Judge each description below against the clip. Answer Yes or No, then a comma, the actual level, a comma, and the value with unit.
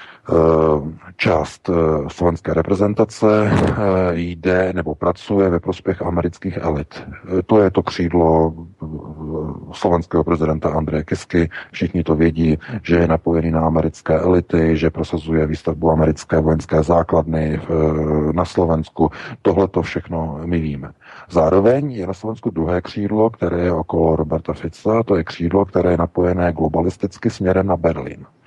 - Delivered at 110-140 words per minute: Yes, average, 130 wpm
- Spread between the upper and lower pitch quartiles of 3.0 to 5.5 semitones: No, narrow, 2.5 semitones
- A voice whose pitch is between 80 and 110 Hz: Yes, very low, 85 Hz